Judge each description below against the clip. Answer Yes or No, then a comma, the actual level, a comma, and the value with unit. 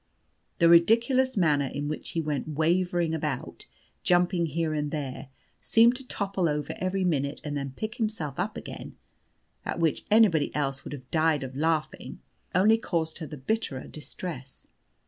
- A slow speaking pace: No, average, 160 wpm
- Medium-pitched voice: Yes, medium, 160 Hz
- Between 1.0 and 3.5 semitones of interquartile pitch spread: No, average, 4.1 semitones